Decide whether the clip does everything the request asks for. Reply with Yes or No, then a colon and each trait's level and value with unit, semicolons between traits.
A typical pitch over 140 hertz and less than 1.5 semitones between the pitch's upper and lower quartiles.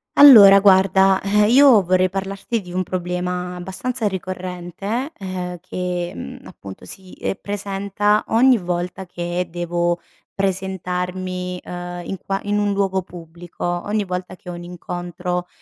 No: medium, 185 Hz; narrow, 1.8 semitones